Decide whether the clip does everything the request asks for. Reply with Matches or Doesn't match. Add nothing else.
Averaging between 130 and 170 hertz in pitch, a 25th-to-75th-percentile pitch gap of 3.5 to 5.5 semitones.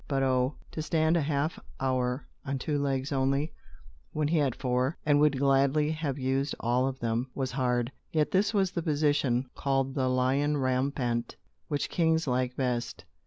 Doesn't match